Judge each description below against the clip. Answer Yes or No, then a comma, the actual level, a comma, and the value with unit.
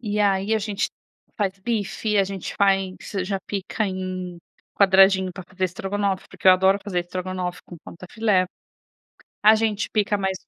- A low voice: No, high, 195 Hz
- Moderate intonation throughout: No, narrow, 1.7 semitones